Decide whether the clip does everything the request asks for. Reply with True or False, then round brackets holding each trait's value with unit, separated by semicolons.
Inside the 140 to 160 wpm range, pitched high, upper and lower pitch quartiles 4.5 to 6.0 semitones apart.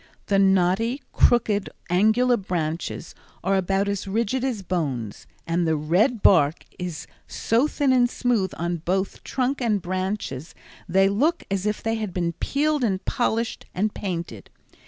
True (150 wpm; 195 Hz; 4.8 semitones)